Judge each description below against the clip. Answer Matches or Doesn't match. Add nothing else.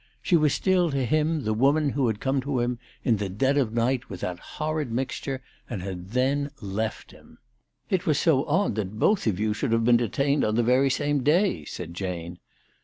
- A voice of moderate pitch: Doesn't match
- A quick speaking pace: Matches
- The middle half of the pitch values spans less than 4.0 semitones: Doesn't match